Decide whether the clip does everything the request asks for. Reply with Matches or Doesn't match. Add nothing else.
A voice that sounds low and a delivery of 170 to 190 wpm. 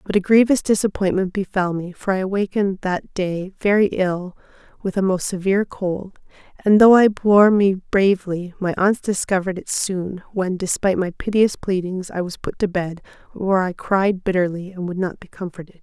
Doesn't match